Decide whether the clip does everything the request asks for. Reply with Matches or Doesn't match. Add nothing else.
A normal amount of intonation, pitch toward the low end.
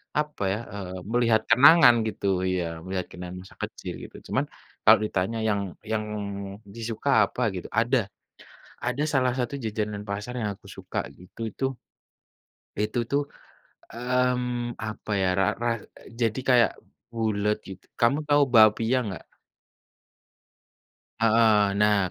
Matches